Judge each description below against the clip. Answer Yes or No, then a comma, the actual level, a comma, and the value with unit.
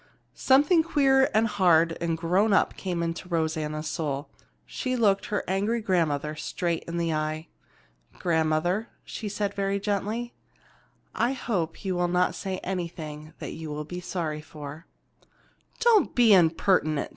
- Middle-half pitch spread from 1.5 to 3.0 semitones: No, average, 4.5 semitones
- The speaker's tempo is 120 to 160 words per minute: Yes, average, 145 wpm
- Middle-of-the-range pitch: Yes, medium, 175 Hz